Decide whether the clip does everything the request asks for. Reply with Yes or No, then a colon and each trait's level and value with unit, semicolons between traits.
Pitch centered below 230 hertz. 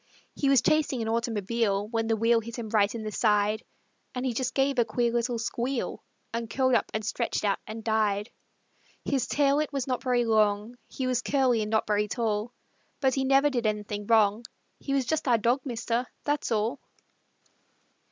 No: high, 235 Hz